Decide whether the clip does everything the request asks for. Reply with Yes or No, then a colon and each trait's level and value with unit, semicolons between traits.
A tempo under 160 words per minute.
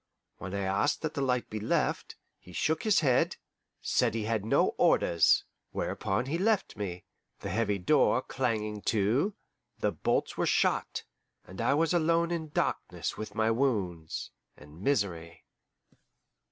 Yes: average, 150 wpm